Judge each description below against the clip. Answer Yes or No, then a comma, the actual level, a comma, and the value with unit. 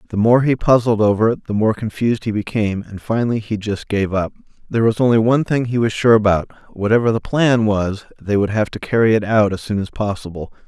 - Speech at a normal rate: No, fast, 230 wpm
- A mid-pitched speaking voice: No, low, 110 Hz